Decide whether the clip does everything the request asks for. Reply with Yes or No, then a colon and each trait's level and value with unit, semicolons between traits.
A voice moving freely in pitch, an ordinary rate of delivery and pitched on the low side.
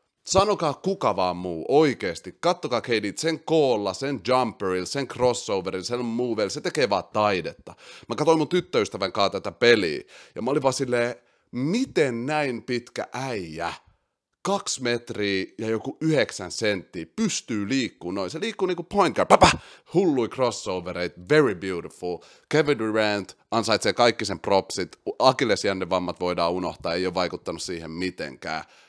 Yes: wide, 8.5 semitones; average, 140 wpm; low, 120 Hz